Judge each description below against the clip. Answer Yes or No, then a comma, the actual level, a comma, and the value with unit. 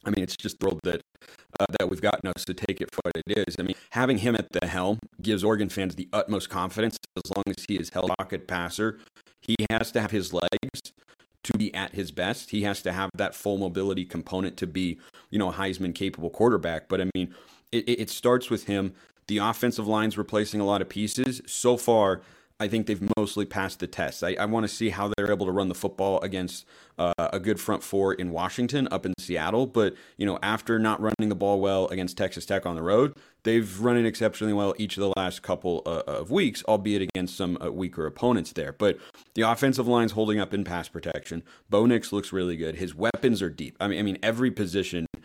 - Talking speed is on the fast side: Yes, fast, 230 wpm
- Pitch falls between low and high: No, low, 100 Hz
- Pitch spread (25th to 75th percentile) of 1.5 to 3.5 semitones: Yes, average, 2.9 semitones